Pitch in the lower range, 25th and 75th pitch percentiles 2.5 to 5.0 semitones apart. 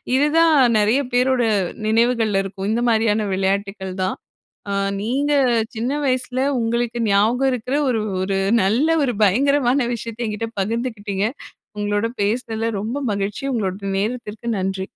No: high, 225 Hz; average, 3.7 semitones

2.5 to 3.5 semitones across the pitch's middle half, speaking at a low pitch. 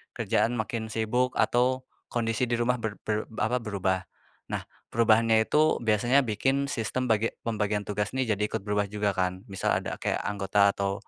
Yes: average, 2.8 semitones; low, 110 Hz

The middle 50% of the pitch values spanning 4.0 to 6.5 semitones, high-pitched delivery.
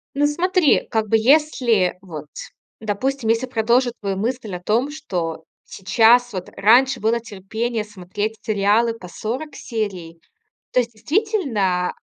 Yes: average, 4.4 semitones; high, 225 Hz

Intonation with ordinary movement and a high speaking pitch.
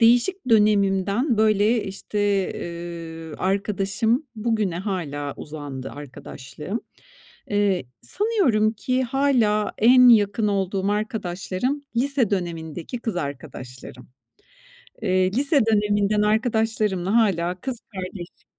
Yes: average, 4.3 semitones; high, 205 Hz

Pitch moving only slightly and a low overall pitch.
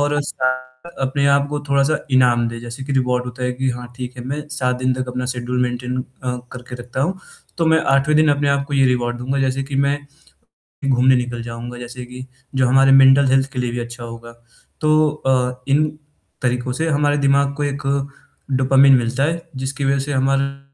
Yes: narrow, 2.1 semitones; low, 130 Hz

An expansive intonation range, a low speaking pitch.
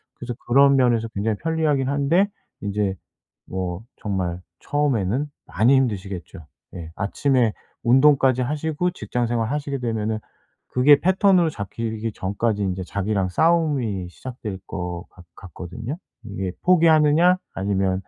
Yes: wide, 6.6 semitones; low, 115 Hz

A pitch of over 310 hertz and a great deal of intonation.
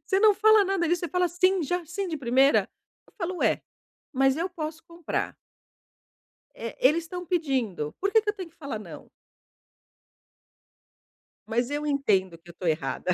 Yes: very high, 325 Hz; wide, 5.8 semitones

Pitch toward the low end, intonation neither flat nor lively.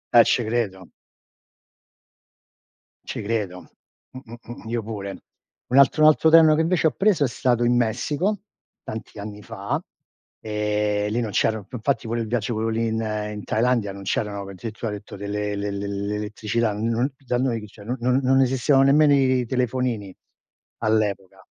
Yes: low, 115 Hz; average, 3.4 semitones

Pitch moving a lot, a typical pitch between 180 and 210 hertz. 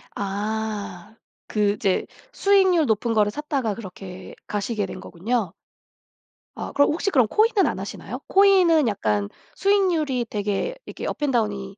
No: wide, 7.6 semitones; high, 220 Hz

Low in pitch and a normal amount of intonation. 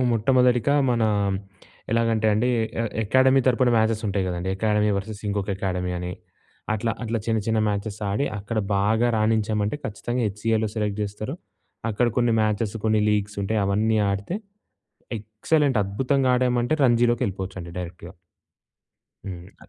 Yes: low, 110 Hz; average, 3.0 semitones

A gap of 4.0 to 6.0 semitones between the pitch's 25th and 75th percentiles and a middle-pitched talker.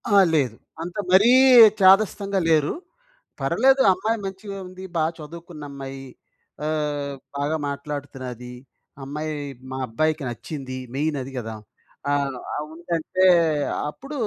Yes: average, 4.9 semitones; medium, 155 Hz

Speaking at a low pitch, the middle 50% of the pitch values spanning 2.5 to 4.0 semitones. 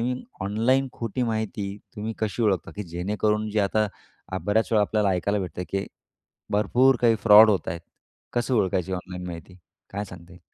Yes: low, 105 Hz; average, 2.9 semitones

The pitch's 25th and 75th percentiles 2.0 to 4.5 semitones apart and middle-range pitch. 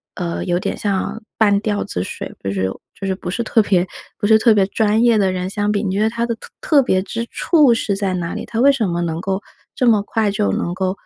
No: average, 3.2 semitones; high, 205 Hz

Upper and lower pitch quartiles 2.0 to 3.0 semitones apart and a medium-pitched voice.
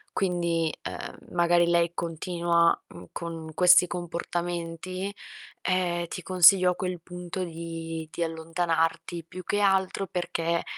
No: narrow, 1.5 semitones; medium, 175 Hz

